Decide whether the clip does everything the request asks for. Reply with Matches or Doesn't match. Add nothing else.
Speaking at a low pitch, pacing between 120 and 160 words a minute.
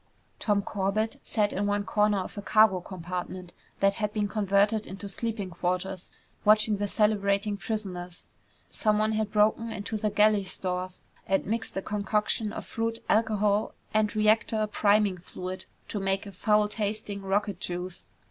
Doesn't match